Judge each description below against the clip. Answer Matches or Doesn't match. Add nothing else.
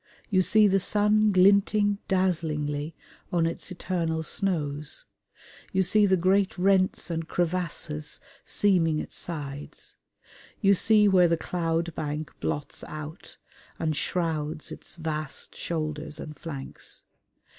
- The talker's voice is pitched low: Doesn't match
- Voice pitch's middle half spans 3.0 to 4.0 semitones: Matches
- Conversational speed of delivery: Doesn't match